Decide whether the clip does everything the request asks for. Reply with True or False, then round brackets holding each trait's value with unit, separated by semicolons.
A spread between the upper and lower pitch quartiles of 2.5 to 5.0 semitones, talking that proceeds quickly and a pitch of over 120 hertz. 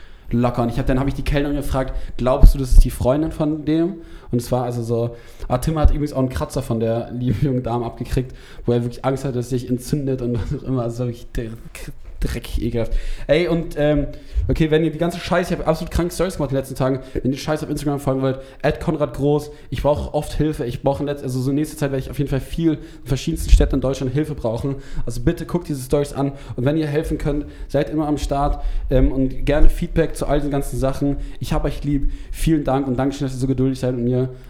True (2.8 semitones; 255 wpm; 140 Hz)